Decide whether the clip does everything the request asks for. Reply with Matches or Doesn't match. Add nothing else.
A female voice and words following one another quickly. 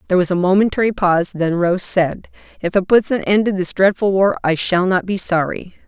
Matches